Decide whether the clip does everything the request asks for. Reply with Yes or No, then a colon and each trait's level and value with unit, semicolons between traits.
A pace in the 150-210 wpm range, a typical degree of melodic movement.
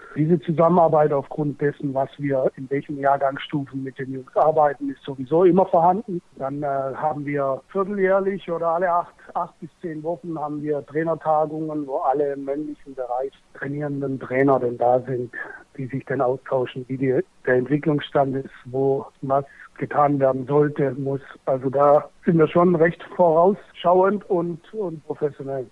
Yes: average, 155 wpm; average, 3.3 semitones